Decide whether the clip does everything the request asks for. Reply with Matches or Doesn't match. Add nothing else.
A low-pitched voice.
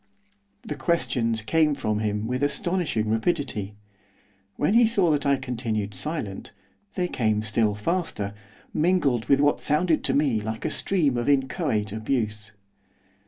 Matches